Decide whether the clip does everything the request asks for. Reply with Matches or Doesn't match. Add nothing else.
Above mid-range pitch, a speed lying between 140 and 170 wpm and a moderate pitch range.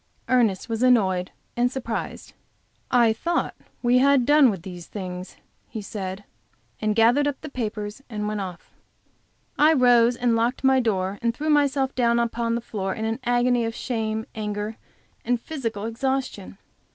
Matches